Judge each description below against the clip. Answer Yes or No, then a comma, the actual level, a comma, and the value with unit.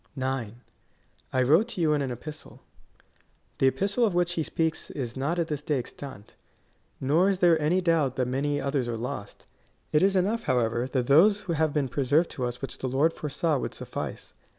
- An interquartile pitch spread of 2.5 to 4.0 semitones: No, average, 4.4 semitones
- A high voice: No, medium, 145 Hz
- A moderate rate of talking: Yes, average, 195 wpm